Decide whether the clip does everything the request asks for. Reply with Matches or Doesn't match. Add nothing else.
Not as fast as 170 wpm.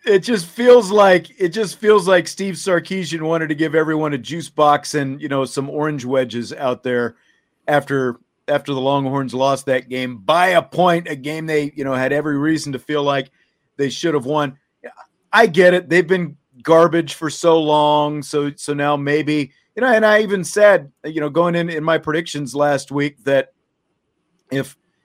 Doesn't match